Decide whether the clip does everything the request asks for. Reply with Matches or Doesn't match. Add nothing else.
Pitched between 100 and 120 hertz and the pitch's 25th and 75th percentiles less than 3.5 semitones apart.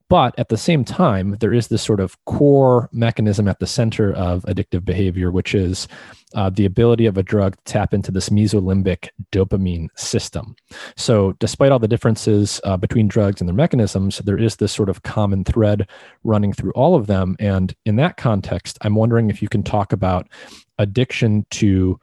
Matches